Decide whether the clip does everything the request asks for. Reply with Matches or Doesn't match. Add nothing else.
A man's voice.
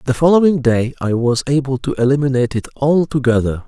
Matches